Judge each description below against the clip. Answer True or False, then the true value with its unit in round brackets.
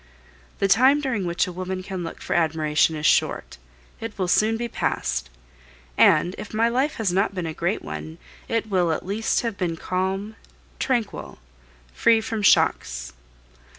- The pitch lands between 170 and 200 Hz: True (190 Hz)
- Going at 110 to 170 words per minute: True (165 wpm)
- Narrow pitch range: False (5.1 semitones)